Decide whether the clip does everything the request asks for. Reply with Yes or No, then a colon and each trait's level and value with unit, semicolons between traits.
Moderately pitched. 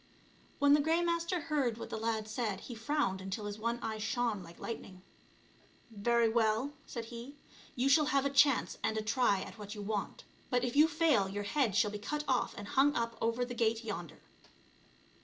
No: high, 230 Hz